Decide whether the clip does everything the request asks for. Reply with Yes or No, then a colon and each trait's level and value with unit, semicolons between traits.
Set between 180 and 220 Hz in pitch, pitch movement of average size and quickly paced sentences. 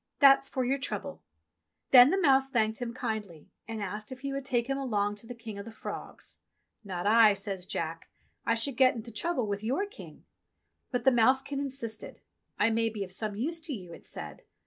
No: high, 230 Hz; average, 4.4 semitones; fast, 210 wpm